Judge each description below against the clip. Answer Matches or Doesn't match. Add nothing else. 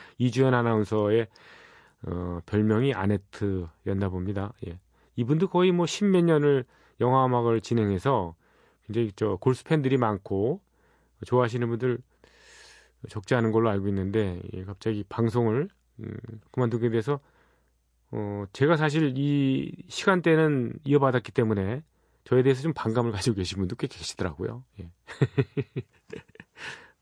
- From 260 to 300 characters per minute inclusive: Matches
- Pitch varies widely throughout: Doesn't match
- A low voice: Matches